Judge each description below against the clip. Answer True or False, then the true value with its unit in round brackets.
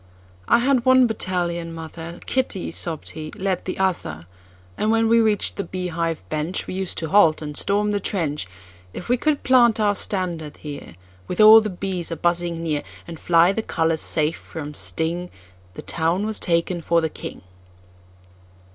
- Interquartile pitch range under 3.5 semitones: False (4.5 semitones)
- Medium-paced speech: True (155 wpm)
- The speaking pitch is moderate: True (170 Hz)